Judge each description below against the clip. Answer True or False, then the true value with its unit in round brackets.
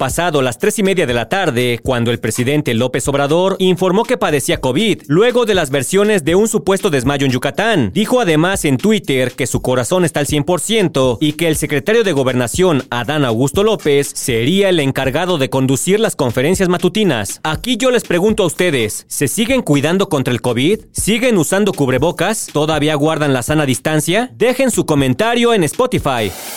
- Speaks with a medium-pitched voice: True (155 Hz)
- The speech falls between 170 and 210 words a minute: True (180 wpm)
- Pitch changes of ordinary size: False (6.4 semitones)